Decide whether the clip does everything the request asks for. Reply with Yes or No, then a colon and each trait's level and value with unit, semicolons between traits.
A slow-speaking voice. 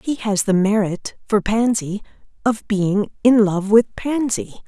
Yes: slow, 130 wpm